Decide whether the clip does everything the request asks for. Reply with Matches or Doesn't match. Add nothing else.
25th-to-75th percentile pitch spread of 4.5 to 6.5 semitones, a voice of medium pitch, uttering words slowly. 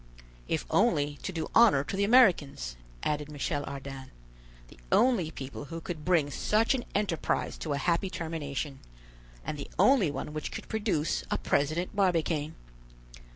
Doesn't match